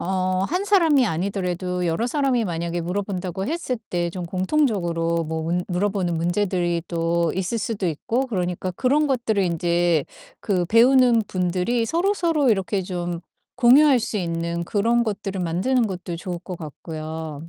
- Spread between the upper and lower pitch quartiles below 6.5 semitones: Yes, average, 5.3 semitones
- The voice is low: No, medium, 185 Hz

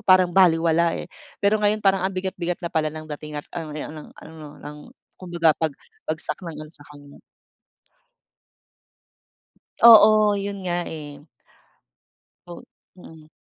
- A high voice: No, medium, 170 Hz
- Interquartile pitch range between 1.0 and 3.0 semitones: No, average, 3.7 semitones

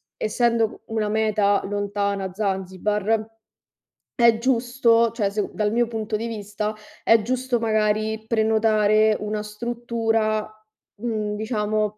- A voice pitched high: Yes, high, 215 Hz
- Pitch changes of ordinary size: No, narrow, 1.5 semitones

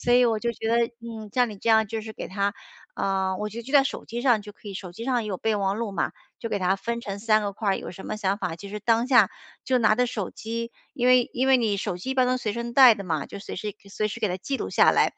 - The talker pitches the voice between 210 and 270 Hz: Yes, high, 220 Hz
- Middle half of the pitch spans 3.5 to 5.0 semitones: No, average, 2.9 semitones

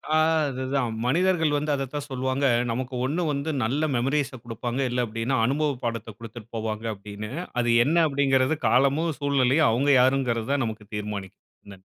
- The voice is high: No, low, 130 Hz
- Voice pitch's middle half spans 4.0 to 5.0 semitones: No, average, 3.6 semitones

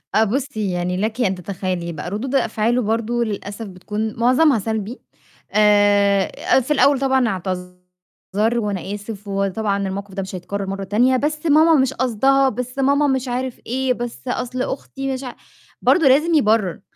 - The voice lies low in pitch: No, high, 220 Hz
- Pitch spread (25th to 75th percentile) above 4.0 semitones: Yes, average, 4.7 semitones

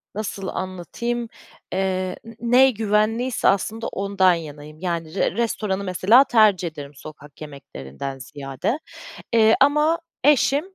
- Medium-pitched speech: No, high, 195 Hz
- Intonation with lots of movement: Yes, wide, 6.6 semitones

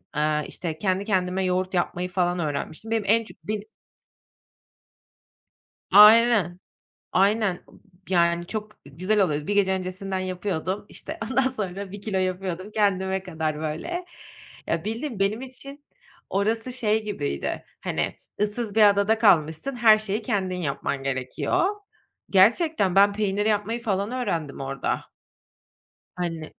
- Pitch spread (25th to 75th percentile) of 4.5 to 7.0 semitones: No, average, 3.5 semitones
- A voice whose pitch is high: Yes, high, 195 Hz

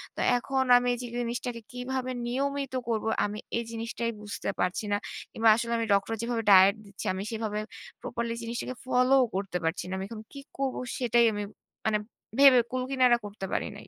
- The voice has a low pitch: No, high, 235 Hz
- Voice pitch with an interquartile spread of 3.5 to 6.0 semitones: No, average, 3.1 semitones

